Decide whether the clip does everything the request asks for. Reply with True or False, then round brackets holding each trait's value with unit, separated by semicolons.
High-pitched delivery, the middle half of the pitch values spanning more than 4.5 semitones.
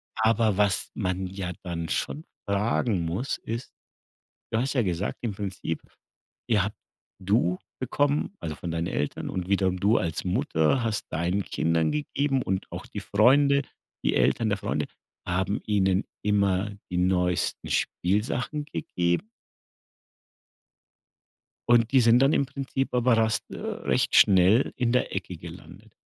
False (105 Hz; 4.9 semitones)